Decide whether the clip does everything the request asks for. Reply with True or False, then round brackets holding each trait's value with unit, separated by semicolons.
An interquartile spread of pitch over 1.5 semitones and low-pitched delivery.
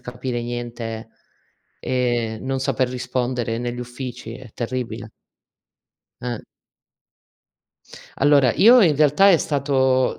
True (2.0 semitones; 125 Hz)